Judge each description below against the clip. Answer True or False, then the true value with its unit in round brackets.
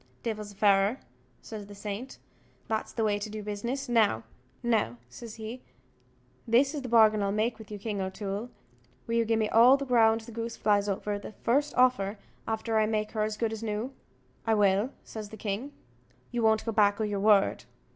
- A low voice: False (220 Hz)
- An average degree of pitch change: False (2.0 semitones)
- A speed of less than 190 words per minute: False (195 wpm)